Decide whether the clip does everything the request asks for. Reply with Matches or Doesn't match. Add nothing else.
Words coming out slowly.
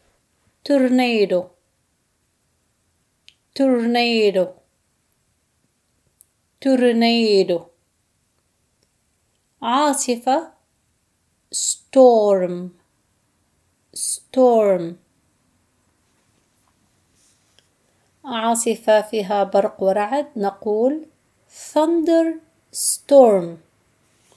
Matches